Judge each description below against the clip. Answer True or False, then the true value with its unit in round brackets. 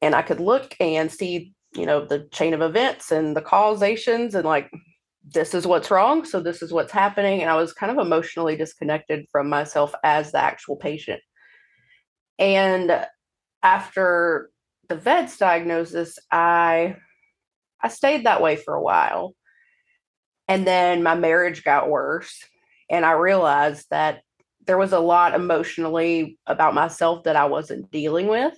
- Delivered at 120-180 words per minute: True (155 wpm)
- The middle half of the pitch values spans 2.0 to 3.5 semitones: True (3.2 semitones)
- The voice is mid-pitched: True (170 Hz)